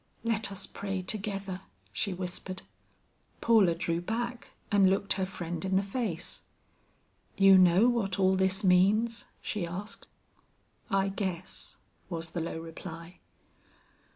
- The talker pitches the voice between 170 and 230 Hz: Yes, high, 190 Hz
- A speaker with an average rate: No, slow, 125 wpm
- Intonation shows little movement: Yes, narrow, 2.2 semitones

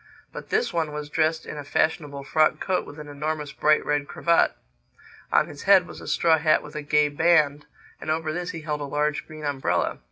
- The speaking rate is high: Yes, fast, 215 wpm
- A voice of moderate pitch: Yes, medium, 150 Hz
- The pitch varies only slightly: Yes, narrow, 1.5 semitones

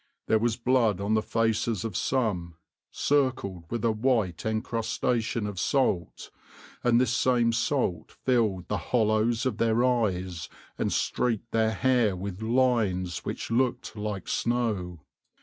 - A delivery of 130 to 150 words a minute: Yes, slow, 135 wpm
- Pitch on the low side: Yes, low, 110 Hz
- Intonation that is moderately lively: Yes, average, 3.4 semitones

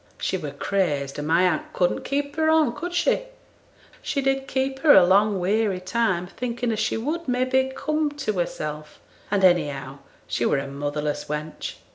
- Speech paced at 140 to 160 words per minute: No, average, 180 wpm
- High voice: Yes, high, 205 Hz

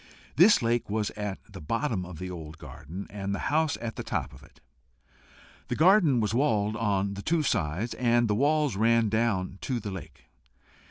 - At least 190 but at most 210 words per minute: Yes, average, 195 wpm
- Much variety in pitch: No, average, 4.2 semitones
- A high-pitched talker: No, low, 110 Hz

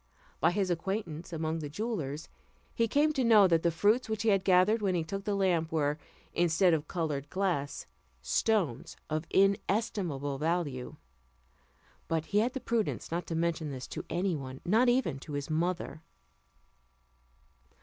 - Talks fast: No, average, 160 wpm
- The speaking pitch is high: No, medium, 175 Hz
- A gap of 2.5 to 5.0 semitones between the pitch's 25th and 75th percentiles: Yes, average, 4.7 semitones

